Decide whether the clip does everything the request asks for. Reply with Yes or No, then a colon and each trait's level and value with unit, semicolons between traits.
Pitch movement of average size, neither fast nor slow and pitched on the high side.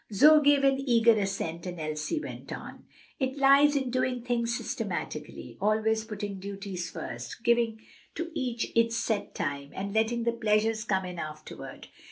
Yes: average, 4.3 semitones; average, 160 wpm; high, 225 Hz